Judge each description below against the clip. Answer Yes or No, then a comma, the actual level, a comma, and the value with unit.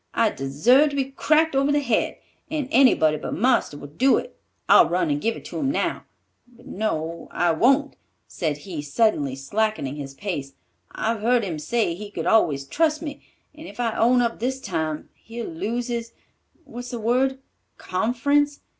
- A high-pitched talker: Yes, high, 230 Hz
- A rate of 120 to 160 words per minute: No, average, 170 wpm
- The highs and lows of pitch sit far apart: Yes, wide, 8.2 semitones